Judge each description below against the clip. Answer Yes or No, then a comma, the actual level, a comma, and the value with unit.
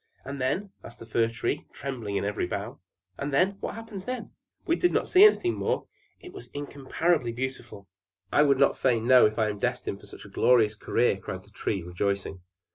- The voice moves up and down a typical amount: No, wide, 5.9 semitones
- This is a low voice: Yes, low, 125 Hz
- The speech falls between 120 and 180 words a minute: No, average, 200 wpm